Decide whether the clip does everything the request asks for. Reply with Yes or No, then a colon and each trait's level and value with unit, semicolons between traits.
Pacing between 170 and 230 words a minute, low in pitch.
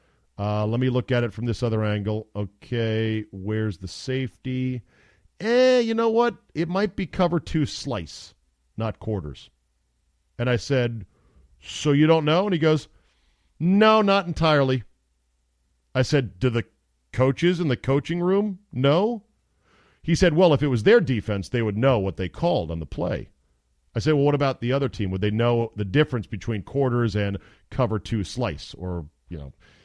Yes: average, 175 wpm; low, 115 Hz